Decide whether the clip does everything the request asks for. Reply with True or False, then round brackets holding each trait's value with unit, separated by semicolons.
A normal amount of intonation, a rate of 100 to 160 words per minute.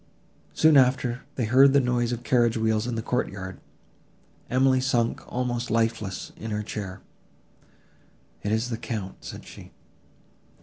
False (2.3 semitones; 140 wpm)